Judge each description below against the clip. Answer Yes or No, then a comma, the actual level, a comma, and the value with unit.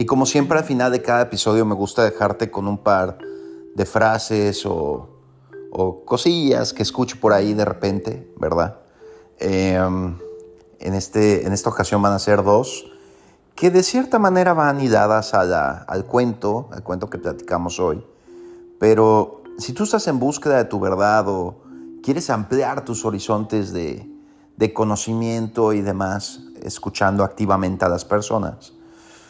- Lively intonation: No, average, 4.3 semitones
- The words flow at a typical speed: Yes, average, 155 wpm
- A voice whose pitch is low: Yes, low, 105 Hz